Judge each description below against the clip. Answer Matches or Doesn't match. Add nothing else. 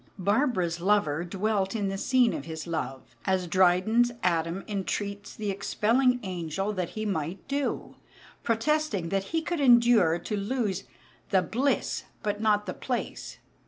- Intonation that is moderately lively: Matches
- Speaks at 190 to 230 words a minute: Doesn't match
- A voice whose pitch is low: Doesn't match